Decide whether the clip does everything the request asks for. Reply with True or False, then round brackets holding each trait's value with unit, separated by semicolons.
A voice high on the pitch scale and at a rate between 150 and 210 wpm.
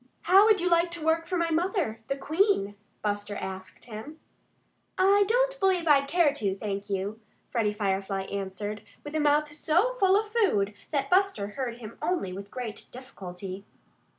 True (275 Hz; 170 wpm)